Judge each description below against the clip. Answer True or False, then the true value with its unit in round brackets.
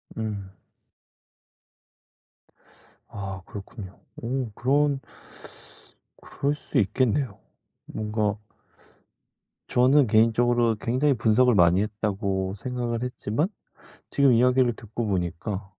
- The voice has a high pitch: False (115 Hz)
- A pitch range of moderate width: True (3.6 semitones)